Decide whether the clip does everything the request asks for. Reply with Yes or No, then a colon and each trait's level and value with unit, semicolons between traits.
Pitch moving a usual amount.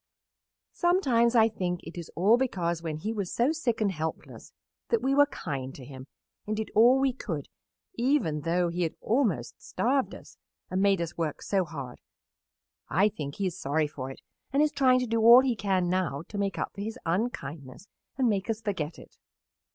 No: wide, 6.6 semitones